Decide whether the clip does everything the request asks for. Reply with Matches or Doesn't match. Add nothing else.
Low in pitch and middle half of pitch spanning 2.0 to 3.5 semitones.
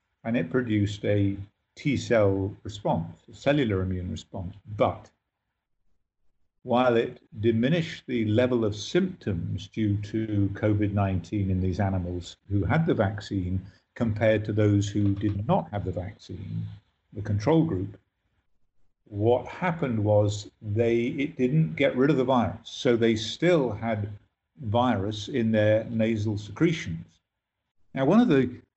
Matches